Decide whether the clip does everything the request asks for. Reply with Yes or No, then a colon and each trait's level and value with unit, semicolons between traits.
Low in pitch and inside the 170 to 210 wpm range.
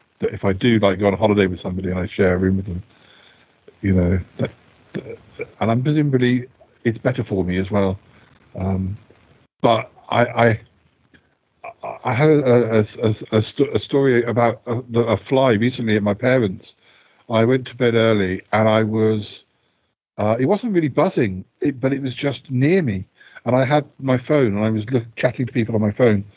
Yes: low, 115 Hz; average, 200 wpm